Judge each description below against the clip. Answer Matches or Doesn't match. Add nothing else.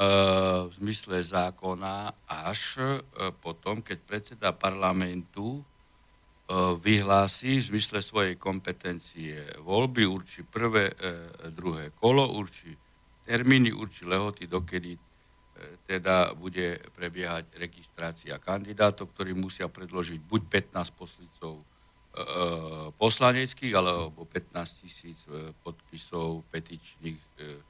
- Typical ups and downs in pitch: Matches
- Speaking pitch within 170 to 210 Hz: Doesn't match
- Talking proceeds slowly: Matches